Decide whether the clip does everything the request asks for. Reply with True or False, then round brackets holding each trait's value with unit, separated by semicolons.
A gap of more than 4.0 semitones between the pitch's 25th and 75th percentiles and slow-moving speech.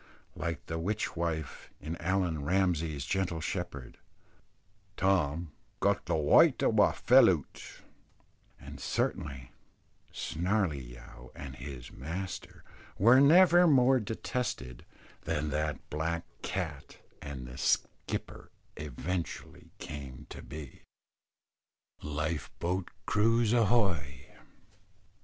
True (4.9 semitones; 100 wpm)